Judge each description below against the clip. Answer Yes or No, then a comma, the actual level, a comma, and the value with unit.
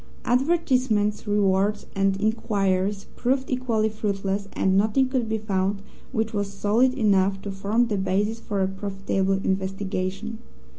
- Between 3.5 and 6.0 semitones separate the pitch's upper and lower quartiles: No, narrow, 2.5 semitones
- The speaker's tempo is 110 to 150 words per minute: Yes, slow, 135 wpm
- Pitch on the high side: Yes, high, 205 Hz